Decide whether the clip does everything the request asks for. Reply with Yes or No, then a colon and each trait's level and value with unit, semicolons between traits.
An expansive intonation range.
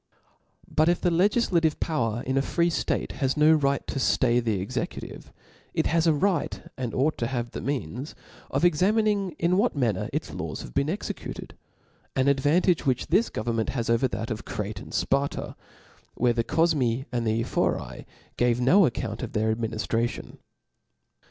Yes: wide, 5.9 semitones